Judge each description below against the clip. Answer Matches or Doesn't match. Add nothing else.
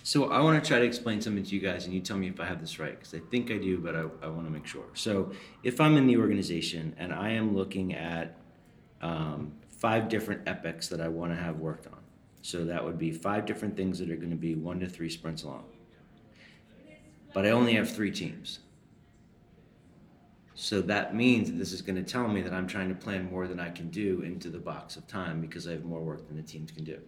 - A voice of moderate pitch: Doesn't match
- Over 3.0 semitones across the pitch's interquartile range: Matches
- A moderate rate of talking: Doesn't match